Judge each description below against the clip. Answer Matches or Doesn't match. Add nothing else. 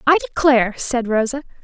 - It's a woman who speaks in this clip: Matches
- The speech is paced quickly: Doesn't match